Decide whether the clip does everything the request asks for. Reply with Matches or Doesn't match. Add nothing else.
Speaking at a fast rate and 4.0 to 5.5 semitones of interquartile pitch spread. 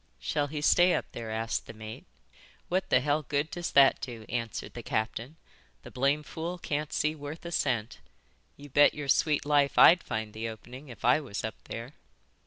Doesn't match